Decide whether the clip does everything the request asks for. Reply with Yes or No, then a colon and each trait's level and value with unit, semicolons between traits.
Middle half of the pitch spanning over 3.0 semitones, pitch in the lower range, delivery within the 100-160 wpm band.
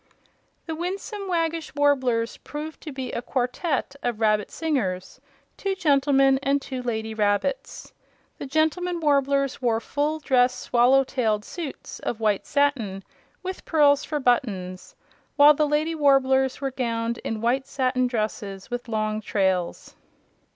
No: average, 4.4 semitones; very high, 265 Hz; slow, 135 wpm